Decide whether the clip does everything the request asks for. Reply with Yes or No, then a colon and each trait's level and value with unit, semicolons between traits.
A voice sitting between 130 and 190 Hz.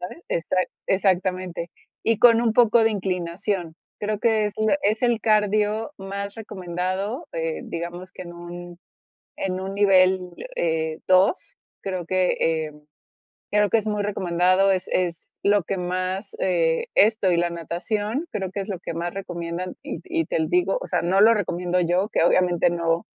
Yes: medium, 185 Hz